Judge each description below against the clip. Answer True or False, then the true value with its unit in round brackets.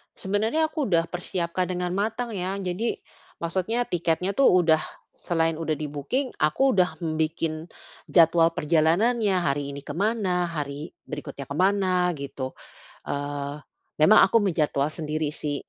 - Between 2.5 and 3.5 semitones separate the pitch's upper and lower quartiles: False (3.9 semitones)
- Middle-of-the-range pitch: True (170 Hz)